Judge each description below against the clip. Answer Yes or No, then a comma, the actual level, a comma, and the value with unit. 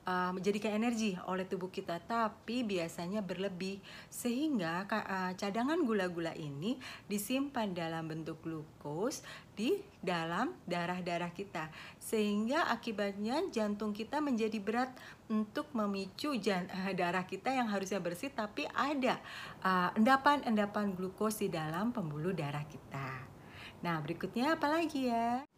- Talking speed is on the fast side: No, average, 110 wpm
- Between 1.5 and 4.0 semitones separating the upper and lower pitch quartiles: No, average, 4.8 semitones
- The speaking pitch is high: Yes, high, 205 Hz